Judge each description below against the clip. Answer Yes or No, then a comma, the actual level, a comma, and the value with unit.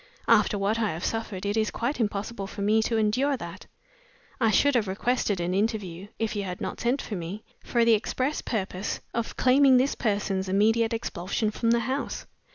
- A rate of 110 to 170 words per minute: No, average, 190 wpm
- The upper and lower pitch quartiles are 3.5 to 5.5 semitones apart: No, average, 3.0 semitones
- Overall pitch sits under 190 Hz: No, high, 215 Hz